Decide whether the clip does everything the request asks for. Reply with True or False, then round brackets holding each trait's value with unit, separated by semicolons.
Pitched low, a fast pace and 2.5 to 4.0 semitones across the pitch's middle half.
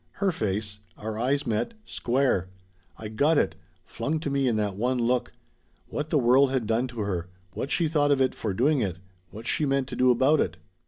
False (125 Hz; 210 wpm; 4.4 semitones)